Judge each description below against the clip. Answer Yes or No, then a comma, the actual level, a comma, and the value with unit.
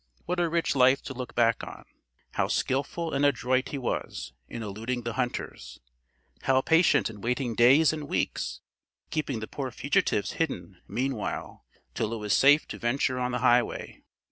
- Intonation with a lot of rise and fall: No, average, 3.4 semitones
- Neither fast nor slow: Yes, average, 170 wpm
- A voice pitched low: Yes, low, 125 Hz